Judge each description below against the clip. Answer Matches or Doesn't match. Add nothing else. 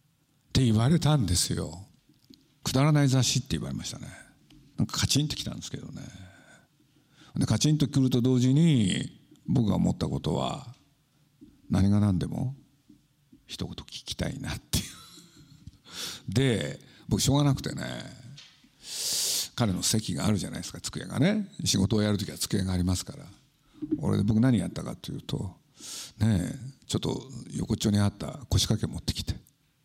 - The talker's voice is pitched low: Matches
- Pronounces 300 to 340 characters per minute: Matches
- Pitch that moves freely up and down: Matches